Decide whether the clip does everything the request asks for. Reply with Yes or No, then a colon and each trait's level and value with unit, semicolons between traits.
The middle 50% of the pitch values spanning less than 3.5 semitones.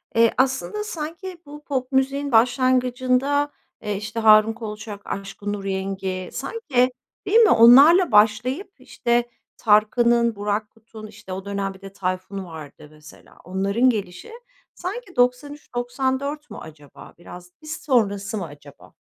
No: average, 5.2 semitones